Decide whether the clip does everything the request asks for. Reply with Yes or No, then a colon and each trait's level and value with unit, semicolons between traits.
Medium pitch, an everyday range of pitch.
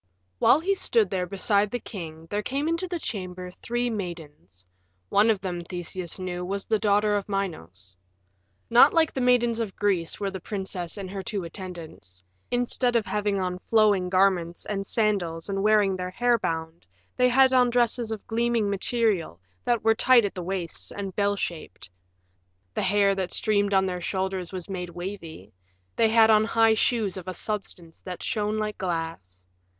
No: high, 195 Hz; average, 3.8 semitones